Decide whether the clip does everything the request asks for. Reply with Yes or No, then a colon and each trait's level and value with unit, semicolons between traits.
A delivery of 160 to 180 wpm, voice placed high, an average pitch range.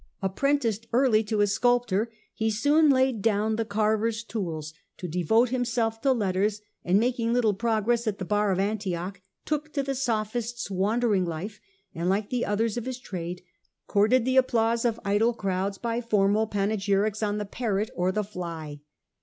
Yes: average, 170 wpm; high, 215 Hz; average, 3.1 semitones